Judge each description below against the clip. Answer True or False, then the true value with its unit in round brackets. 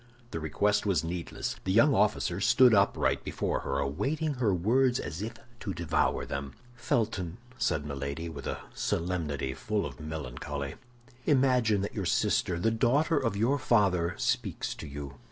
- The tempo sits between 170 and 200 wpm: False (155 wpm)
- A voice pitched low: True (95 Hz)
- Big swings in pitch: True (7.2 semitones)